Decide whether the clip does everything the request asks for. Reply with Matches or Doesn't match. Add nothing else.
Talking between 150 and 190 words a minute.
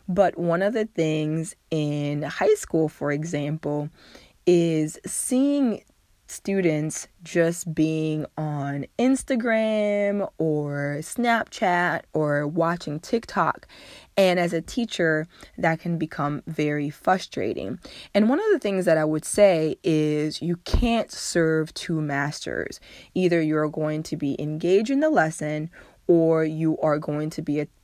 Doesn't match